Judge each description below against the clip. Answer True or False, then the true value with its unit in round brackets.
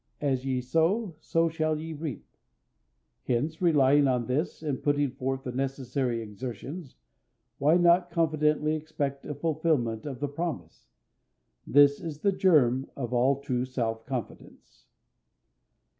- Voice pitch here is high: False (140 Hz)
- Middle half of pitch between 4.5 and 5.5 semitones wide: False (3.6 semitones)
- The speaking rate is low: True (130 wpm)